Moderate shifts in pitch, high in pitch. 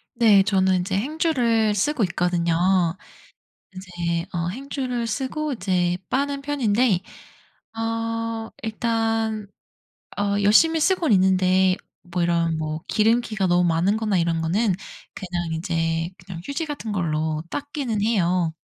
Yes: average, 4.7 semitones; high, 205 Hz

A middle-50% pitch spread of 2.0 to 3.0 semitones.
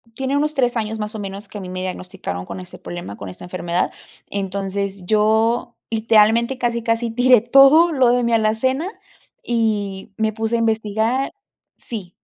No: average, 3.4 semitones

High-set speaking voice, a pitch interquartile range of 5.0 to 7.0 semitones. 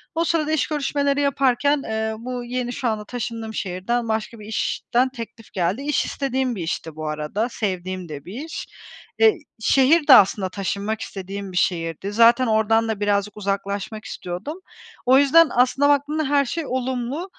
Yes: high, 230 Hz; average, 5.3 semitones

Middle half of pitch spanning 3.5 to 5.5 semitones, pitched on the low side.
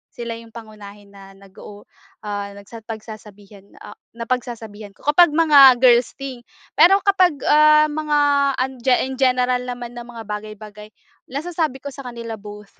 No: average, 4.3 semitones; high, 240 Hz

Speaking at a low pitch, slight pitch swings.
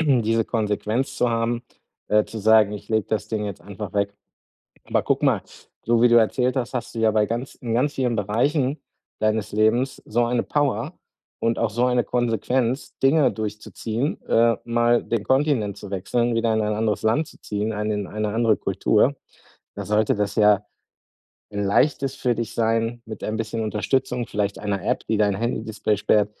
Yes: low, 110 Hz; narrow, 2.3 semitones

